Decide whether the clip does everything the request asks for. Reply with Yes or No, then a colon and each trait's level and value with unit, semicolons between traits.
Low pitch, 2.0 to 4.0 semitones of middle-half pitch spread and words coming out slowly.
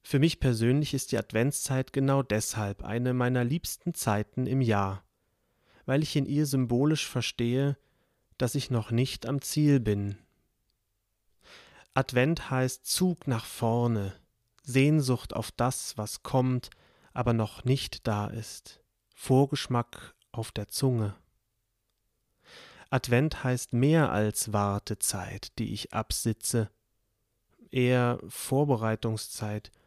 Yes: low, 120 Hz; average, 3.5 semitones; slow, 115 wpm